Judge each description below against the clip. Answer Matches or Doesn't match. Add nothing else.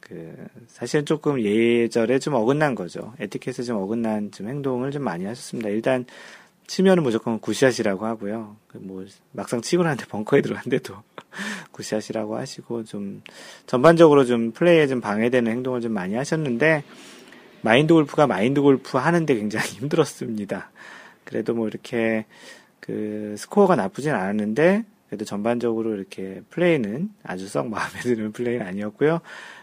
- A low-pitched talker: Matches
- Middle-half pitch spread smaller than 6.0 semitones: Matches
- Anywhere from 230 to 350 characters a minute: Doesn't match